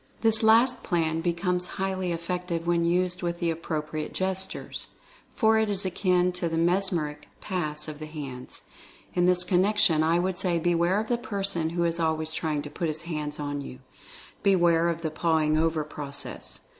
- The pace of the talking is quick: No, average, 180 wpm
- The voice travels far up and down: No, narrow, 2.5 semitones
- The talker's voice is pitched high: No, medium, 170 Hz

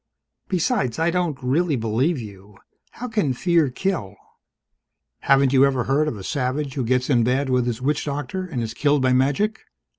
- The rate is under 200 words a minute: Yes, average, 180 wpm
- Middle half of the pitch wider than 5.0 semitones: No, average, 4.2 semitones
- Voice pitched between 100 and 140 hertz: Yes, low, 135 Hz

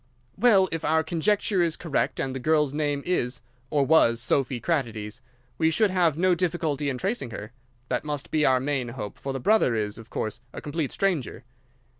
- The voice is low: No, medium, 145 Hz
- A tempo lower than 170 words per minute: No, average, 190 wpm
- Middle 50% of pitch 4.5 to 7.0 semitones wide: Yes, average, 5.0 semitones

